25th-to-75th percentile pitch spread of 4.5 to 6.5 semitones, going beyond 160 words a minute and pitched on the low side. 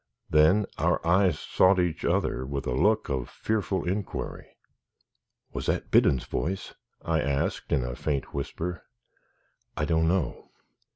No: average, 5.1 semitones; slow, 135 wpm; very low, 80 Hz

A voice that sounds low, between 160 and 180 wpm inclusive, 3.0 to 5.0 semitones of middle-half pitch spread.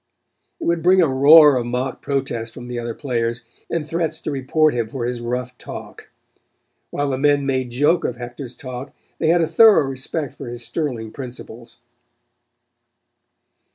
Yes: low, 130 Hz; average, 165 wpm; average, 3.8 semitones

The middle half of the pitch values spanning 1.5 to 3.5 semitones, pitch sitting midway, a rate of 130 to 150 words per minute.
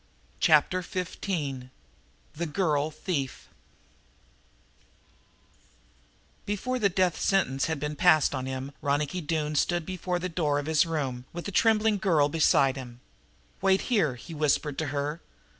No: average, 4.2 semitones; medium, 155 Hz; slow, 135 wpm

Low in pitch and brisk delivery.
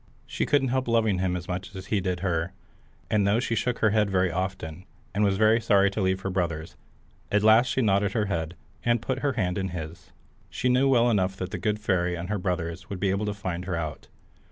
Yes: very low, 95 Hz; fast, 235 wpm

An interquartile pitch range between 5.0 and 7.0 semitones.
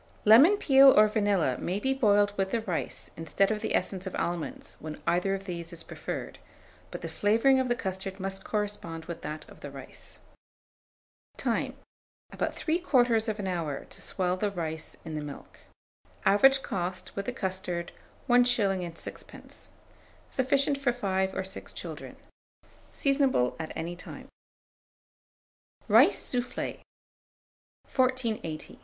Yes: wide, 5.6 semitones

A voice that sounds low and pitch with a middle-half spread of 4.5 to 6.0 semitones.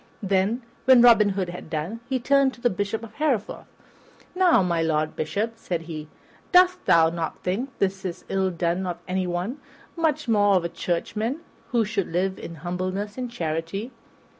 No: high, 195 Hz; average, 5.3 semitones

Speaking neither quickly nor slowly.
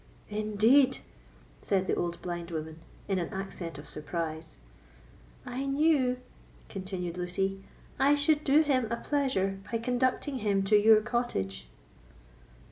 No: slow, 125 wpm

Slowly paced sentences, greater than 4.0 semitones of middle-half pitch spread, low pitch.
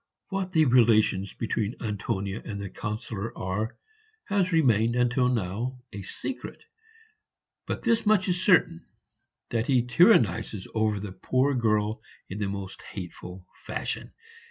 Yes: slow, 130 wpm; average, 4.5 semitones; low, 115 Hz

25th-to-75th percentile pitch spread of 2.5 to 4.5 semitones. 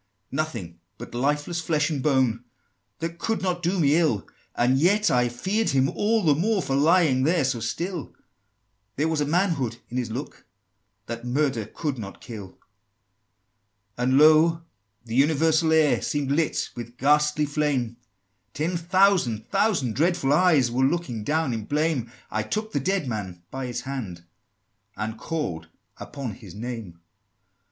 No: average, 5.3 semitones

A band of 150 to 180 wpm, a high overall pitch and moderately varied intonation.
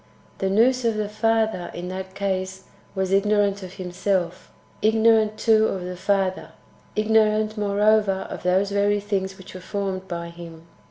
No: average, 155 wpm; high, 200 Hz; narrow, 2.3 semitones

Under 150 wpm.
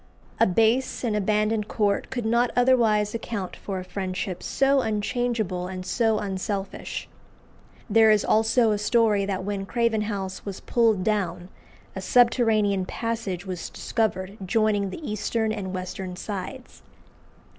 Yes: slow, 135 wpm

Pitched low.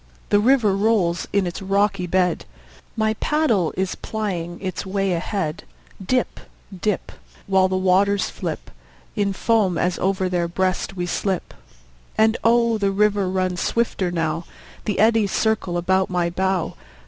No: high, 190 Hz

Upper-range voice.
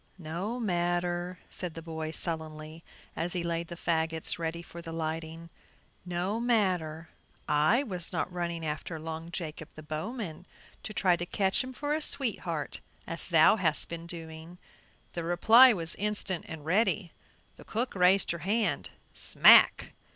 No: medium, 170 Hz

